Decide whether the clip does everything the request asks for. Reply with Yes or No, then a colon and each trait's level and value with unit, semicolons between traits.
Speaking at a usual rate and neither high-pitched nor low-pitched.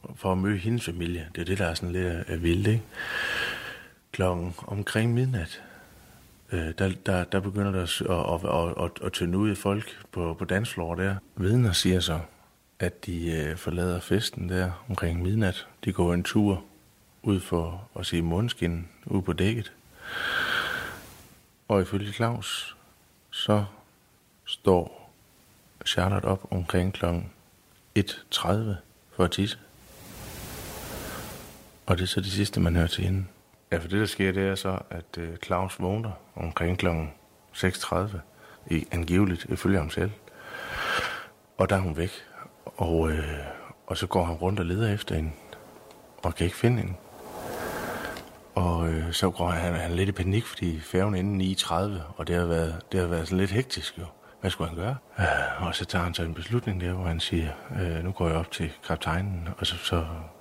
No: average, 170 wpm; very low, 90 Hz